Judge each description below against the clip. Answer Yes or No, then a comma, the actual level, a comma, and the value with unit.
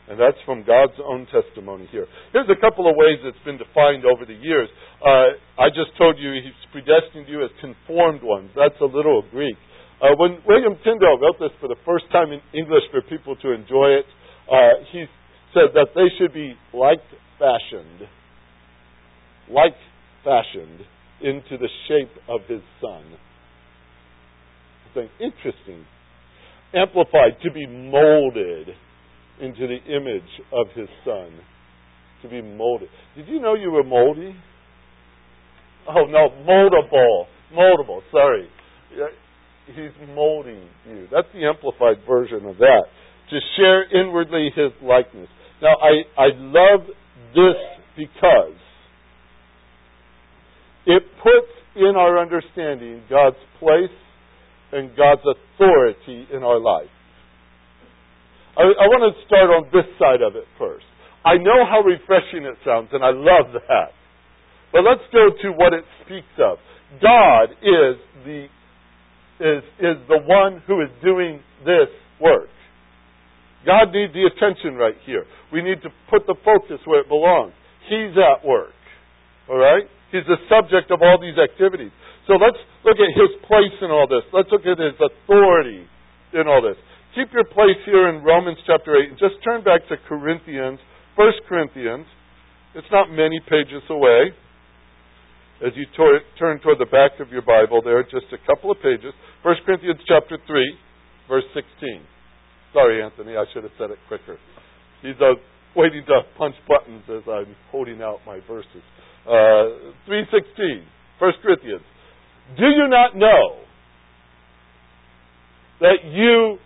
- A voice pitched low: No, medium, 150 Hz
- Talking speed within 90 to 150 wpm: Yes, average, 145 wpm